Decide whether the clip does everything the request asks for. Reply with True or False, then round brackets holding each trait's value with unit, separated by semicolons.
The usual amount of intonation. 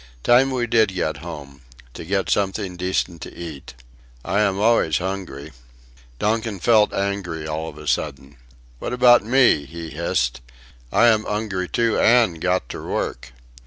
False (5.7 semitones)